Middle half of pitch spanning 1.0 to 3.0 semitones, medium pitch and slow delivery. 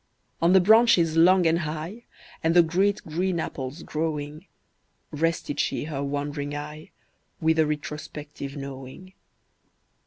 Yes: average, 2.7 semitones; medium, 160 Hz; slow, 125 wpm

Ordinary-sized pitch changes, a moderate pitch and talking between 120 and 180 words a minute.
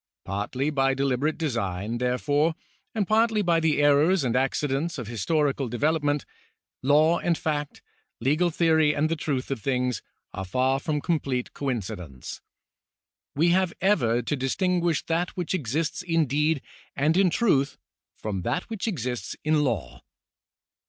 Yes: average, 4.5 semitones; medium, 145 Hz; average, 145 wpm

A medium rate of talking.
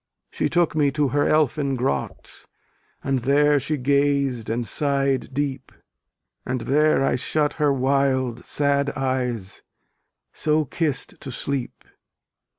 No: slow, 125 wpm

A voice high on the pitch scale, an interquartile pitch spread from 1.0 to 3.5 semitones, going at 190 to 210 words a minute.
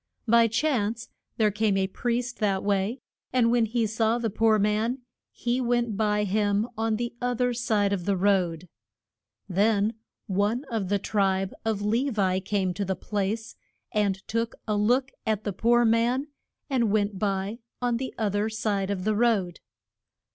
No: high, 215 Hz; average, 2.7 semitones; average, 170 wpm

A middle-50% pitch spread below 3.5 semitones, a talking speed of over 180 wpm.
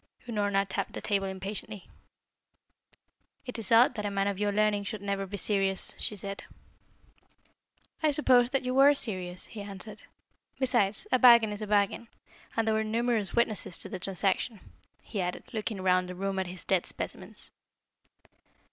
No: narrow, 2.6 semitones; average, 165 wpm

